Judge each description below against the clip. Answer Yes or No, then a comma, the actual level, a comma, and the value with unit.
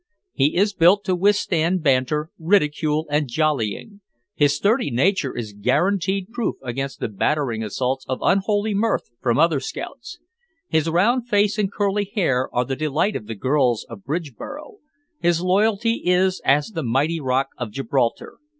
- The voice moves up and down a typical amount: No, wide, 7.1 semitones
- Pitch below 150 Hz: No, medium, 160 Hz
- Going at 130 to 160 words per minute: Yes, average, 155 wpm